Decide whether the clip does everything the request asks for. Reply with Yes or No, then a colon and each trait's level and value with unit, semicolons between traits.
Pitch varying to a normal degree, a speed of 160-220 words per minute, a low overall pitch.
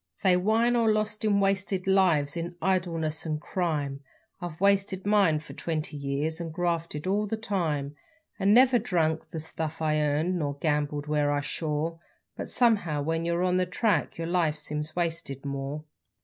No: average, 4.0 semitones; average, 175 wpm; medium, 165 Hz